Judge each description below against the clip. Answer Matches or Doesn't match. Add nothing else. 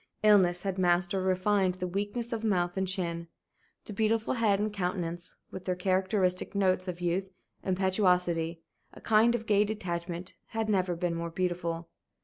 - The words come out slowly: Doesn't match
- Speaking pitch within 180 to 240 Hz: Matches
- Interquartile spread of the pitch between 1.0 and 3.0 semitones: Matches